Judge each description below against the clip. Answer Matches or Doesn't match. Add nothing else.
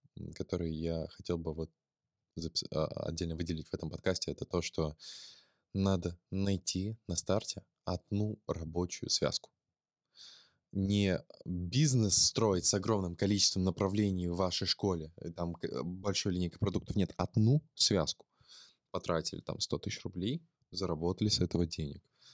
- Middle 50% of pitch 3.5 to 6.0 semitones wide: Doesn't match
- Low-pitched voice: Matches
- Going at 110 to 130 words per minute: Matches